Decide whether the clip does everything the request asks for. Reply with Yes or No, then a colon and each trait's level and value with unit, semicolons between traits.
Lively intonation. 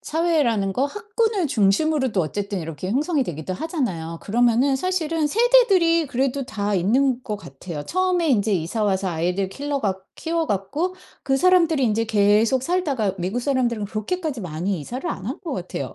Yes: wide, 8.5 semitones